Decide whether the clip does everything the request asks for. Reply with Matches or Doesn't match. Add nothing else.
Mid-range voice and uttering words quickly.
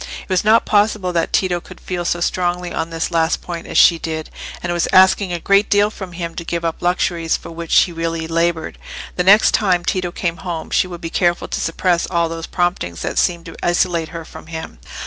Matches